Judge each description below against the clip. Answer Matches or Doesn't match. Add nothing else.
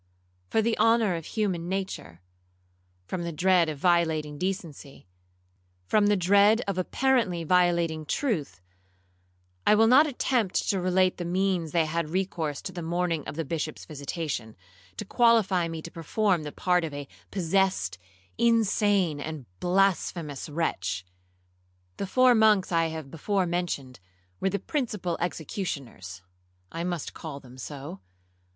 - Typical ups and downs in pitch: Matches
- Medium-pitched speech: Matches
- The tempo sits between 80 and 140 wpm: Matches